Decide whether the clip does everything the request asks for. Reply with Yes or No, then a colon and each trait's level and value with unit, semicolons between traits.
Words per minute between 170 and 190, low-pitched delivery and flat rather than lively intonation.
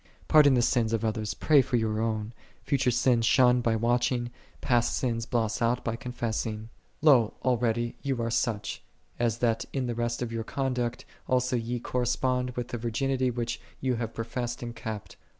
Yes: average, 180 wpm; low, 120 Hz; narrow, 1.7 semitones